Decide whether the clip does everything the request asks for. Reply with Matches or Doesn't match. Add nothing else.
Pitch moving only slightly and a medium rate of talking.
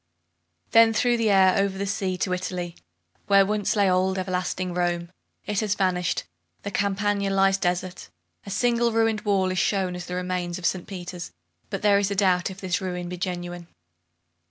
Matches